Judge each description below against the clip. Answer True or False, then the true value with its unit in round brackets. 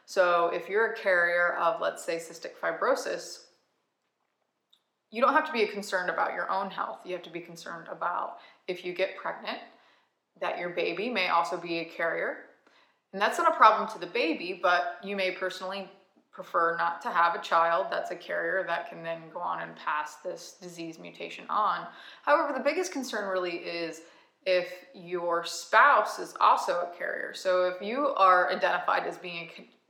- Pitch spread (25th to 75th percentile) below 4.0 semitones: True (3.4 semitones)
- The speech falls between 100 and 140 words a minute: False (185 wpm)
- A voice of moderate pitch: True (180 Hz)